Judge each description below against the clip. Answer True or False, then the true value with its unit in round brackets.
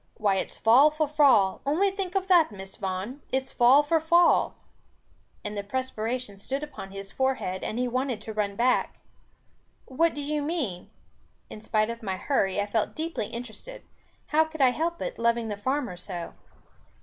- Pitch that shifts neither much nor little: False (6.3 semitones)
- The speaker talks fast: False (175 wpm)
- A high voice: True (250 Hz)